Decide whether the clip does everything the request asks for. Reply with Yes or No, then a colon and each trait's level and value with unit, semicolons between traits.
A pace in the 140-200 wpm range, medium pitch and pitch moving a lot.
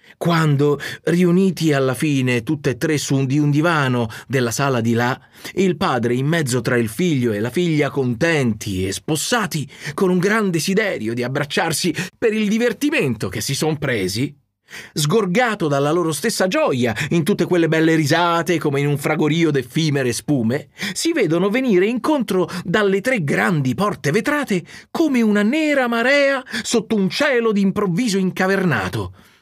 Yes: average, 155 wpm; medium, 160 Hz; wide, 6.2 semitones